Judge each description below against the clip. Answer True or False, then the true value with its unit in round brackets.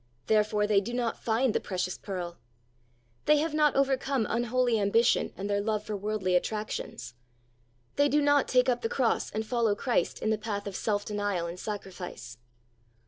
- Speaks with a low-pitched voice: False (215 Hz)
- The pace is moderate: True (175 wpm)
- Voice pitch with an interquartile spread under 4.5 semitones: True (3.4 semitones)